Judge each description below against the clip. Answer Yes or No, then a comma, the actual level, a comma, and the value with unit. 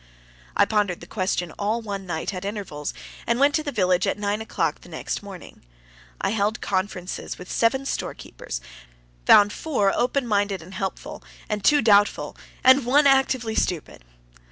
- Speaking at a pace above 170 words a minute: No, average, 155 wpm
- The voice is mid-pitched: No, high, 205 Hz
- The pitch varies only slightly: No, average, 4.1 semitones